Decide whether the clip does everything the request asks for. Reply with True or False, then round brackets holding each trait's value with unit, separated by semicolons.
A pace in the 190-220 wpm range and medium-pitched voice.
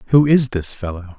False (205 wpm; 110 Hz)